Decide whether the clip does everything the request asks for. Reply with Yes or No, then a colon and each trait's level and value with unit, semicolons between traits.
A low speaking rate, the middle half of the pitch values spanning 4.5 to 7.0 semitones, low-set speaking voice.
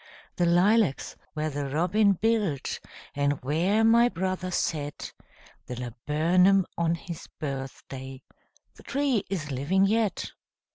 No: slow, 115 wpm; wide, 5.5 semitones; medium, 170 Hz